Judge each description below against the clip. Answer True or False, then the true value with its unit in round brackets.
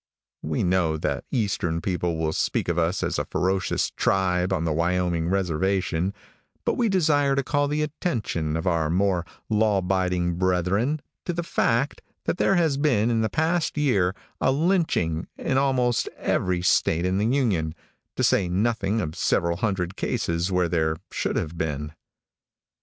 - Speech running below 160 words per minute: False (165 wpm)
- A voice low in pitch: True (95 Hz)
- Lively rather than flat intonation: True (6.7 semitones)